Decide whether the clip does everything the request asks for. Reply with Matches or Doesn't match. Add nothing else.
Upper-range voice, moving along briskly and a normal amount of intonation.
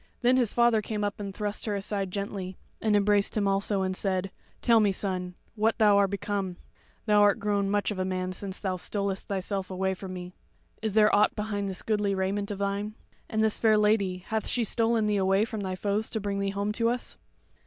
Doesn't match